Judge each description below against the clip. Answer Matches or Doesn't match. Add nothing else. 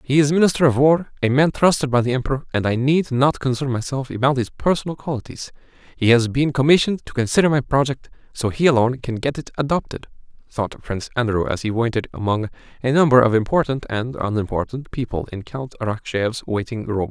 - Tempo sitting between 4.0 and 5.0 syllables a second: Doesn't match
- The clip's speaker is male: Matches